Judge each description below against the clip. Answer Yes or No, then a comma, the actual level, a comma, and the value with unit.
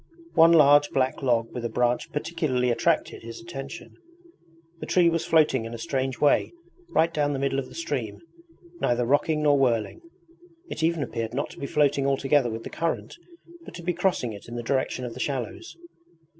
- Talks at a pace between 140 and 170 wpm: No, average, 190 wpm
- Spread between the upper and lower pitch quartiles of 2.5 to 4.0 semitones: No, average, 4.4 semitones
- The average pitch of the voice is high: No, medium, 140 Hz